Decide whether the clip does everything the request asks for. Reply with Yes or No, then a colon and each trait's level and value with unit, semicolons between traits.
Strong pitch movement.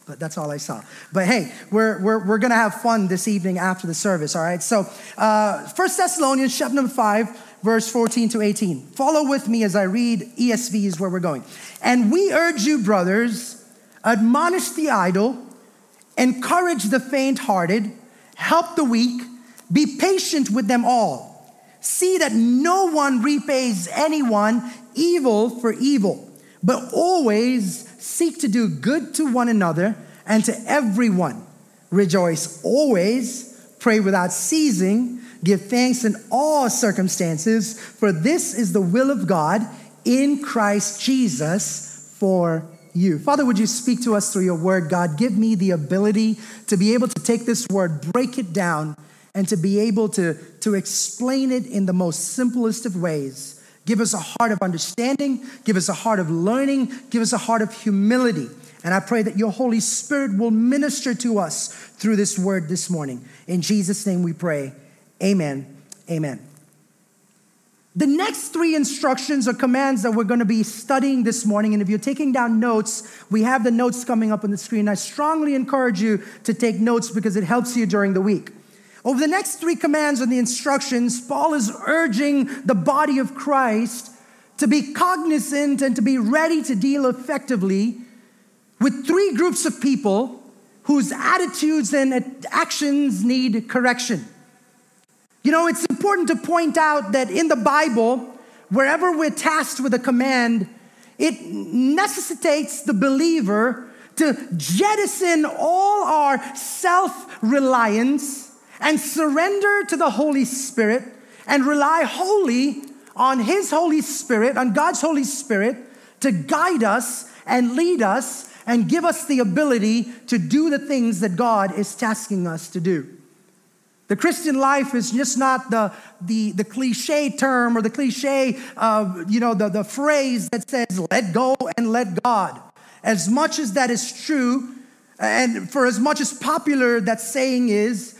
No: average, 4.7 semitones